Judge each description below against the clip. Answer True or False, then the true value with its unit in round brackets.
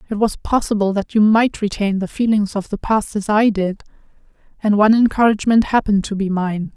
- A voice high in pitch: True (210 Hz)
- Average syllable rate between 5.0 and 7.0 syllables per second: True (5.7 syllables/s)